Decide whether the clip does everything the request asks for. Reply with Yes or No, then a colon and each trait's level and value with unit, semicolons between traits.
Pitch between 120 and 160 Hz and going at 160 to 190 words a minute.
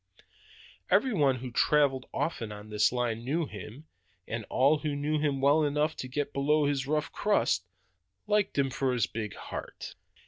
Yes: medium, 140 Hz; average, 170 wpm